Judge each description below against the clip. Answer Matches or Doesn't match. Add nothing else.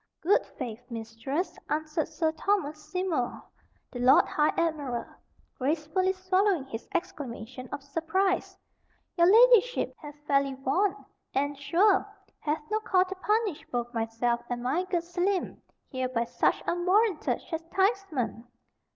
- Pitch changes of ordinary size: Doesn't match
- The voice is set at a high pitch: Matches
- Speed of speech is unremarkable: Doesn't match